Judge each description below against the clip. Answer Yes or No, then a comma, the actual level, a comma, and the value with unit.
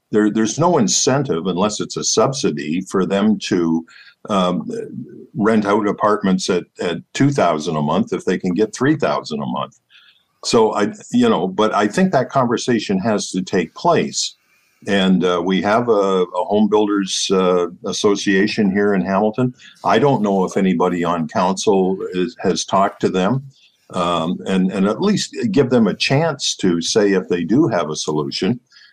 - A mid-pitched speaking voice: No, low, 100 Hz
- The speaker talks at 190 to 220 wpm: No, average, 170 wpm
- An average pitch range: Yes, average, 3.2 semitones